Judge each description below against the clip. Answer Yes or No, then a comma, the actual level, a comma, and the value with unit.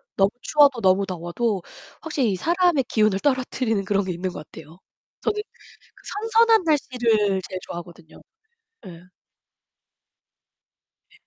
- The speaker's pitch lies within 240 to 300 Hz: No, high, 215 Hz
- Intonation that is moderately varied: No, wide, 7.7 semitones